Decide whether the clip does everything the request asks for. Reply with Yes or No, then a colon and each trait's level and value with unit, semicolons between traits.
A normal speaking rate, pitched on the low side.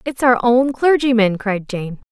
No: average, 170 wpm; high, 235 Hz